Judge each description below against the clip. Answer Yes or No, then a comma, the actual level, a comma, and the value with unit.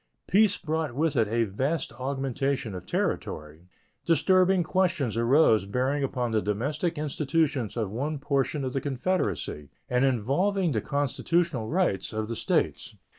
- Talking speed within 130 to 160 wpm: Yes, average, 140 wpm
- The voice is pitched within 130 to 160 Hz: Yes, low, 135 Hz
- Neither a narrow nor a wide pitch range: No, wide, 5.7 semitones